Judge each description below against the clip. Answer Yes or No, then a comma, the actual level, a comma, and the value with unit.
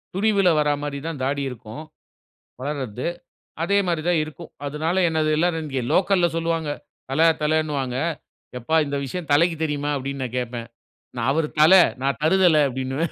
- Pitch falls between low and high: Yes, medium, 150 Hz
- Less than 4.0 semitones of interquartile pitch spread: Yes, average, 3.5 semitones